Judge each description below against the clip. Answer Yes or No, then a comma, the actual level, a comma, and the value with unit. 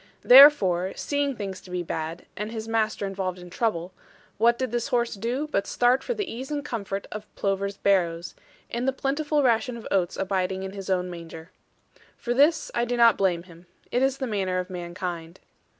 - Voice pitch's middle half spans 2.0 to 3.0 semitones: No, average, 5.0 semitones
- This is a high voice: Yes, high, 200 Hz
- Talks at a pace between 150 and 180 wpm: No, average, 195 wpm